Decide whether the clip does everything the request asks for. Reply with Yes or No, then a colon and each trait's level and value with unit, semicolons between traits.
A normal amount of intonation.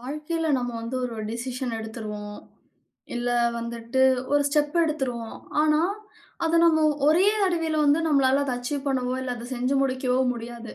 Yes: average, 3.9 semitones